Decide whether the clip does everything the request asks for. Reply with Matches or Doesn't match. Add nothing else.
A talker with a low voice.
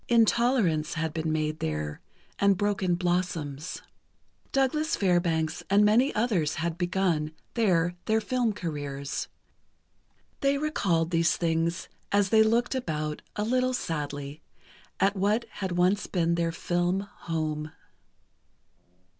Doesn't match